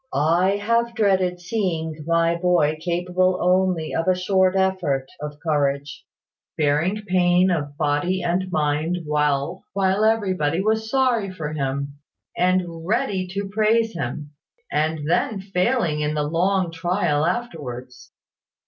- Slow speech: Yes, slow, 130 wpm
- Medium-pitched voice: Yes, medium, 175 Hz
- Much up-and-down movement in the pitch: No, average, 4.0 semitones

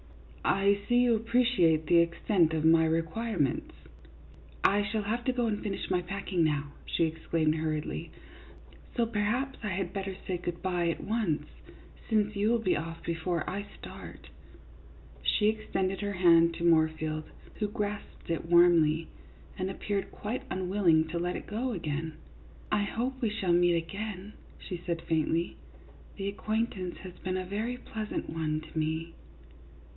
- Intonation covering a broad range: No, average, 4.3 semitones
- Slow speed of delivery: No, average, 165 wpm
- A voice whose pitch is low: No, medium, 185 Hz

